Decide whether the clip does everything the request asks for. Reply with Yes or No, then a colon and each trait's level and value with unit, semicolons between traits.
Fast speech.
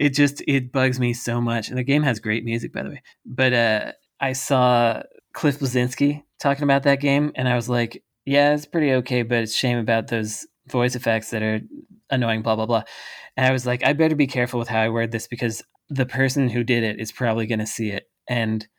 Yes: fast, 230 wpm